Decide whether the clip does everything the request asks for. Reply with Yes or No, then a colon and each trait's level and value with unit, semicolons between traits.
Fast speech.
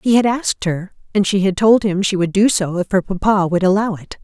Yes: fast, 270 wpm